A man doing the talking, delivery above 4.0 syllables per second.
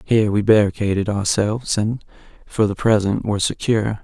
Yes: male; 5.7 syllables/s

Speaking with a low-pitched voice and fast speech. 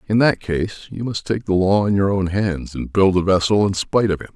Yes: low, 100 Hz; fast, 275 wpm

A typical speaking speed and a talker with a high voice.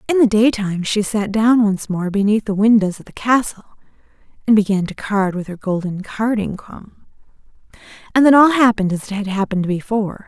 Yes: average, 185 wpm; high, 210 Hz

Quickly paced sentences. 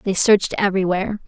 No: average, 140 wpm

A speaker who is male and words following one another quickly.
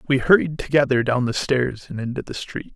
Yes: male; fast, 220 wpm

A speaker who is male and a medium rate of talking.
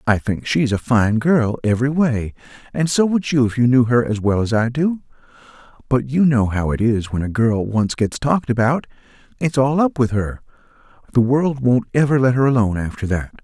No: male; fast, 210 wpm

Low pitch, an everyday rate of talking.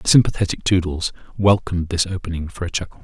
Yes: very low, 90 Hz; average, 180 wpm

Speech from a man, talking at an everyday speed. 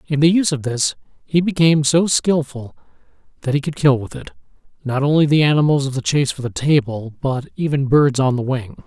No: male; fast, 210 wpm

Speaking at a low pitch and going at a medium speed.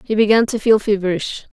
No: high, 210 Hz; average, 195 wpm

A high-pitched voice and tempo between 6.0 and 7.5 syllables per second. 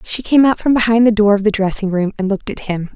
Yes: high, 210 Hz; 6.5 syllables/s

